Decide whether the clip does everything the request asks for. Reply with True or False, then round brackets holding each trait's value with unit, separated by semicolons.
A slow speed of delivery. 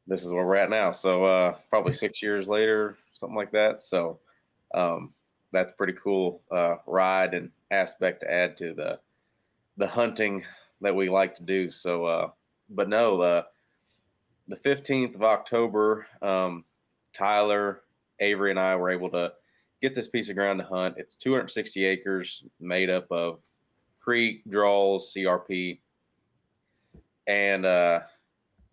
False (145 wpm)